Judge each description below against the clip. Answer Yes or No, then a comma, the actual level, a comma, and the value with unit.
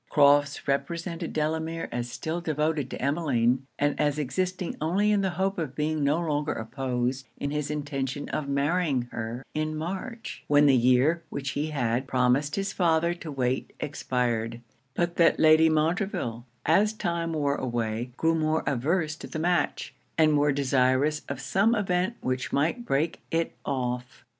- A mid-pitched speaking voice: Yes, medium, 150 Hz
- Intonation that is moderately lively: Yes, average, 3.9 semitones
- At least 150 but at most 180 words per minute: Yes, average, 160 wpm